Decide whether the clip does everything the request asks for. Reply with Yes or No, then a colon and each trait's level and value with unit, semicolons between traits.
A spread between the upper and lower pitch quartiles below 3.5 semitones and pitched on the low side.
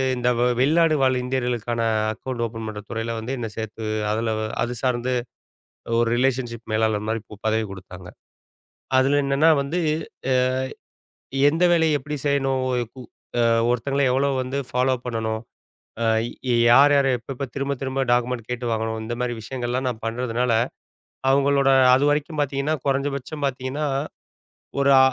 Yes: average, 3.1 semitones; low, 125 Hz